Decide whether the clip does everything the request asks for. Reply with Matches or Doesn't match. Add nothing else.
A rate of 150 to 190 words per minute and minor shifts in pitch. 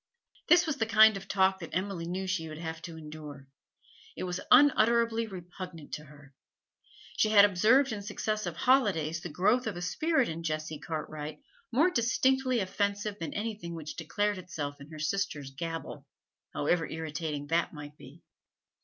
Doesn't match